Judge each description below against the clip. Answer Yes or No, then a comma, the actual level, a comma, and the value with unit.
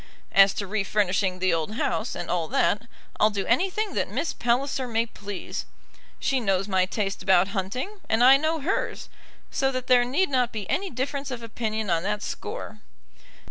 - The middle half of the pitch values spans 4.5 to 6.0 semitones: Yes, average, 5.0 semitones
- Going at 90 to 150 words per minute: No, average, 180 wpm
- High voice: Yes, high, 220 Hz